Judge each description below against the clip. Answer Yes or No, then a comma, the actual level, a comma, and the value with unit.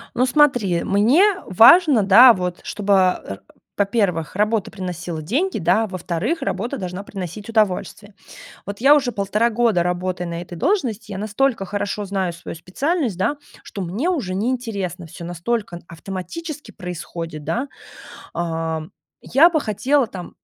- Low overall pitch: No, high, 200 Hz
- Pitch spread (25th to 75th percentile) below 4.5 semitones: No, average, 5.2 semitones